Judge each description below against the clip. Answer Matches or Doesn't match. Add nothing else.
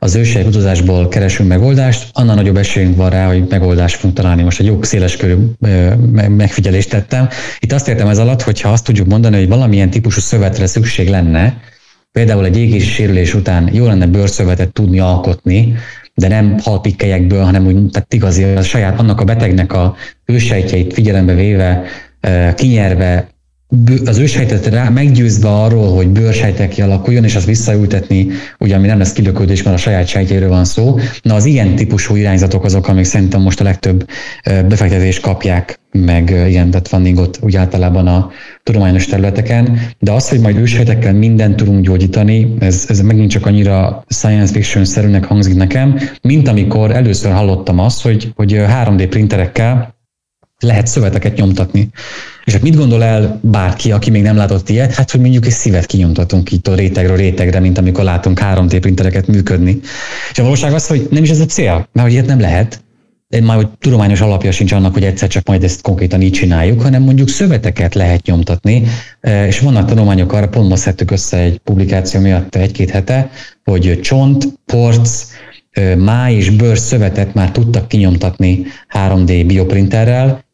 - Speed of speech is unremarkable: Doesn't match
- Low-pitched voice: Matches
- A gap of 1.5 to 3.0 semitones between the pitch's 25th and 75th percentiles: Doesn't match